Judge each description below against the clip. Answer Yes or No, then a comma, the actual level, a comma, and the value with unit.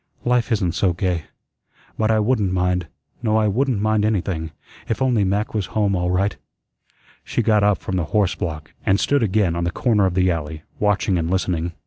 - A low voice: Yes, low, 100 Hz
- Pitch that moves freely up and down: No, average, 3.3 semitones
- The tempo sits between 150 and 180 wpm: No, average, 195 wpm